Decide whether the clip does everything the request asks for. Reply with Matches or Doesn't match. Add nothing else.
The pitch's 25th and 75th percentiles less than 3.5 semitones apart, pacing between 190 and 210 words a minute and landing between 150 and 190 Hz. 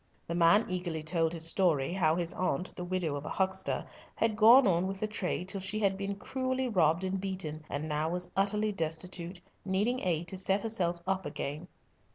Matches